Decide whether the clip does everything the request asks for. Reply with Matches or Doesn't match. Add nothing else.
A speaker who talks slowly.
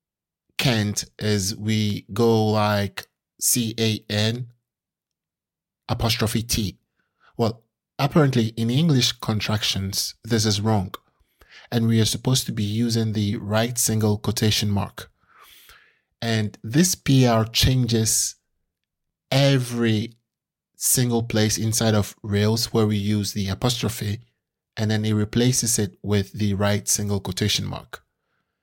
Matches